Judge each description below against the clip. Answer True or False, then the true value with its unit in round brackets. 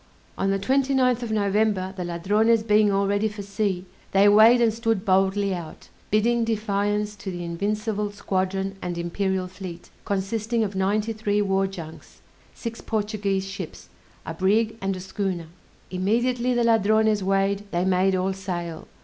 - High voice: True (200 Hz)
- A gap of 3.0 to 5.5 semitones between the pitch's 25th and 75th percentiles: False (2.4 semitones)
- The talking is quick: False (155 wpm)